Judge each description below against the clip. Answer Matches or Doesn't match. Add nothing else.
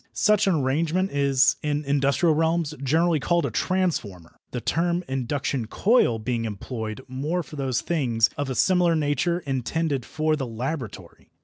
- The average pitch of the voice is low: Doesn't match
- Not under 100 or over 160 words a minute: Matches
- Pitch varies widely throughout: Doesn't match